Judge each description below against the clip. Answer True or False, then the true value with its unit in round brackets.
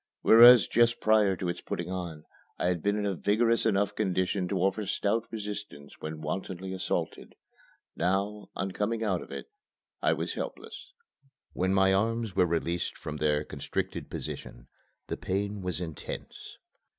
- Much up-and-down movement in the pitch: False (3.0 semitones)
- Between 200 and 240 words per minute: False (155 wpm)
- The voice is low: True (95 Hz)